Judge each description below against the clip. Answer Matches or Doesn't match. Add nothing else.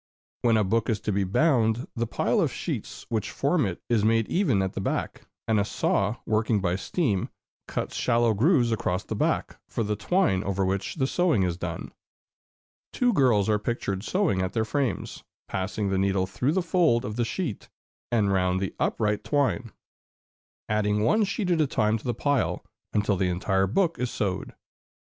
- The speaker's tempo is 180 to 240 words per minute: Matches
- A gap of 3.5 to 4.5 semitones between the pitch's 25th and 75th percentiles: Doesn't match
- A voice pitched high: Doesn't match